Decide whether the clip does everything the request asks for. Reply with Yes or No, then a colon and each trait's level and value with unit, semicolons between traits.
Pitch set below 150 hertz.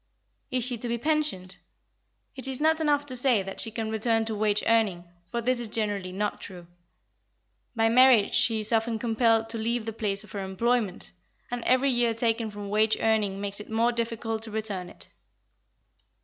No: high, 225 Hz